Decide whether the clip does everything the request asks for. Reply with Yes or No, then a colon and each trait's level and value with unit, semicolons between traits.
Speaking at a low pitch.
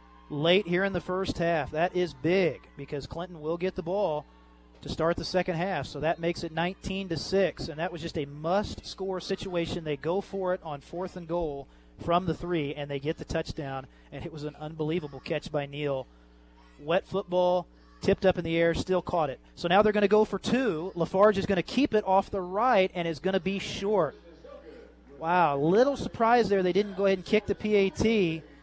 No: medium, 175 Hz